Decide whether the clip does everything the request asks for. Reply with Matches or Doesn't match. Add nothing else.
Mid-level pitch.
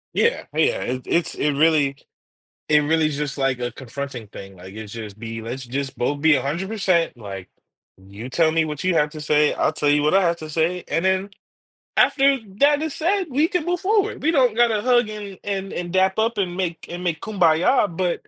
Matches